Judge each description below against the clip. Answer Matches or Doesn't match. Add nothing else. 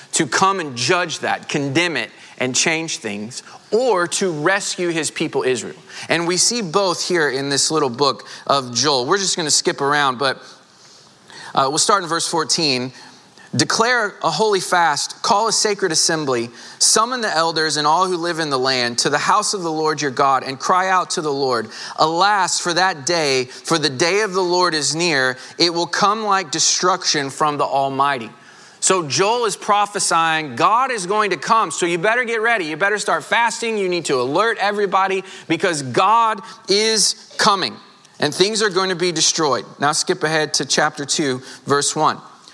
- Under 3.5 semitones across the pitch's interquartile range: Doesn't match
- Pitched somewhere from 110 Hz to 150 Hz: Doesn't match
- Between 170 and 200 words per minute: Matches